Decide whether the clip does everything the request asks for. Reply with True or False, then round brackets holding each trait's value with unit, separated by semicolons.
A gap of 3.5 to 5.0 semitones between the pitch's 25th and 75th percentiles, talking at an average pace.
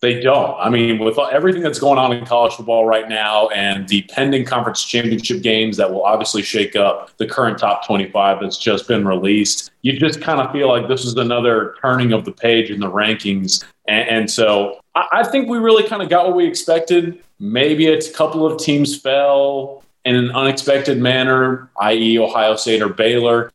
True (4.2 semitones; 195 wpm)